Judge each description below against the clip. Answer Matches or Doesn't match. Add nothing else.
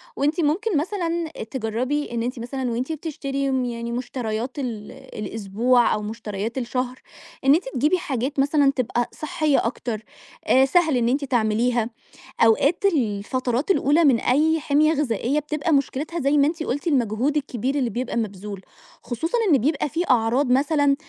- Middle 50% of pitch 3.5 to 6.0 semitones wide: Matches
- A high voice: Matches